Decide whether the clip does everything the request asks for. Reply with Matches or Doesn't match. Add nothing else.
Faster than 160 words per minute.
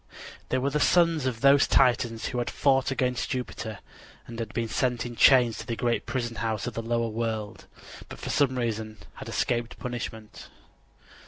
Matches